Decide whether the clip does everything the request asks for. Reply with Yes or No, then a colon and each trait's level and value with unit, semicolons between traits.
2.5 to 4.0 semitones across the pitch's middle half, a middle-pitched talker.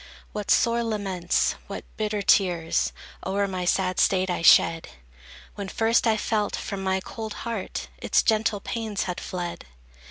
No: average, 2.9 semitones; high, 200 Hz